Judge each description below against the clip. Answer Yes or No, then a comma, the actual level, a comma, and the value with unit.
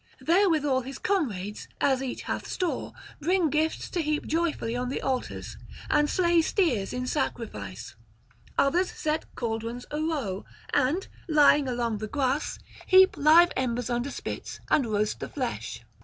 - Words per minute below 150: Yes, average, 140 wpm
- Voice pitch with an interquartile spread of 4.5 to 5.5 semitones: Yes, average, 5.0 semitones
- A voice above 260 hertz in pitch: Yes, very high, 275 Hz